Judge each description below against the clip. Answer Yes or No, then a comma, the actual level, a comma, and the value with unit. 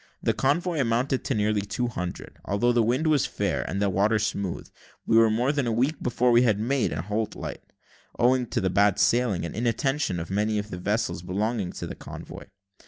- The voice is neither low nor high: No, low, 110 Hz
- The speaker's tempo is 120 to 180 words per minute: No, average, 200 wpm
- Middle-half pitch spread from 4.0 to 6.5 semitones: No, average, 3.5 semitones